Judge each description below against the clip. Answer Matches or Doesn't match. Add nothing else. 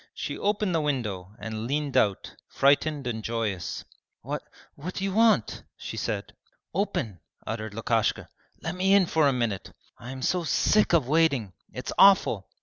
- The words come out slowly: Doesn't match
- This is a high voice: Doesn't match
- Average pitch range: Doesn't match